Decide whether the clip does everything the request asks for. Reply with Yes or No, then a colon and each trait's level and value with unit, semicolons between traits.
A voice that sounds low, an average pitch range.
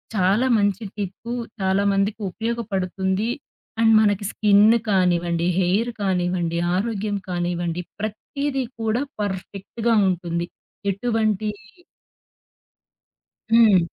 No: high, 200 Hz; average, 3.3 semitones